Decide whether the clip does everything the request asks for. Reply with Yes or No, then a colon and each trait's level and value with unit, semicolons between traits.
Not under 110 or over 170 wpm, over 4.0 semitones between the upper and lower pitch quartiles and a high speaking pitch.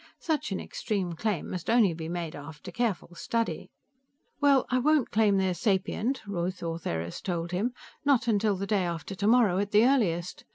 Yes: average, 165 wpm; average, 4.9 semitones; high, 200 Hz